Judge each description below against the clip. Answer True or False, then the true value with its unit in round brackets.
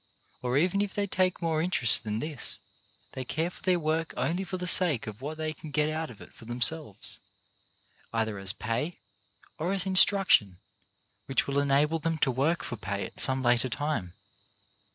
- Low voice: False (150 Hz)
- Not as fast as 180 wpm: False (185 wpm)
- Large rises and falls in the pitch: True (5.7 semitones)